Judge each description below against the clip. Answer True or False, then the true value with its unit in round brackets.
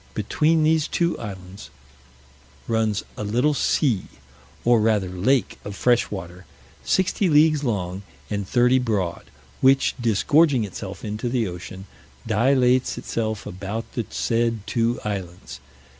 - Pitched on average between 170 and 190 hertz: False (115 Hz)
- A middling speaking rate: False (125 wpm)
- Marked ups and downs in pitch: False (4.8 semitones)